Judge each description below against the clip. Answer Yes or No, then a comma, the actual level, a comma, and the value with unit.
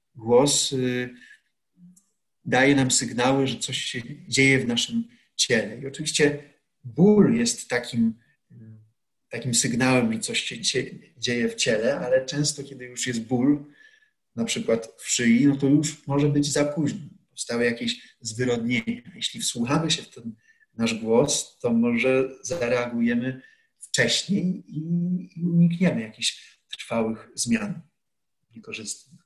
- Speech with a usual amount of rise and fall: No, wide, 6.6 semitones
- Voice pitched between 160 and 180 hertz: No, medium, 140 Hz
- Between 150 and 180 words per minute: No, average, 130 wpm